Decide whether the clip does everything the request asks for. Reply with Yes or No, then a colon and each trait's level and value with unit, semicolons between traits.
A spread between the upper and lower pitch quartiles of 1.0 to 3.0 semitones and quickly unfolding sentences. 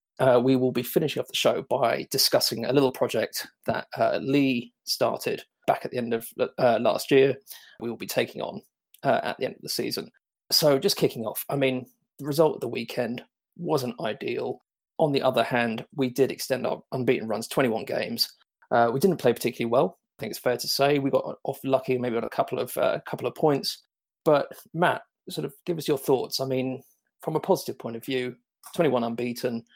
Yes: narrow, 2.4 semitones; fast, 210 wpm